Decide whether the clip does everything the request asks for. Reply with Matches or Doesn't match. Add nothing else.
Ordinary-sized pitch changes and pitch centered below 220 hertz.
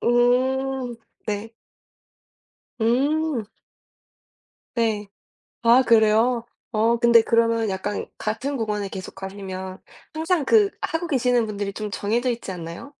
Doesn't match